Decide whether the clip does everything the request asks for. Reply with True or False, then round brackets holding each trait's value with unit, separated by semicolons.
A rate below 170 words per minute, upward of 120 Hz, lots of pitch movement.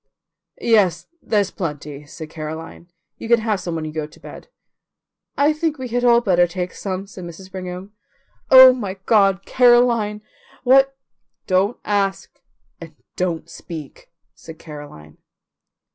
True (145 wpm; 190 Hz; 5.8 semitones)